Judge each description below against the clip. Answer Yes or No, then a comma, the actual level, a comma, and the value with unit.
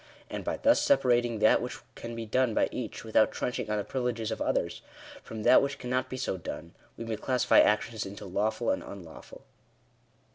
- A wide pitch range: No, average, 2.9 semitones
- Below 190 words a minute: No, average, 195 wpm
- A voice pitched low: Yes, low, 115 Hz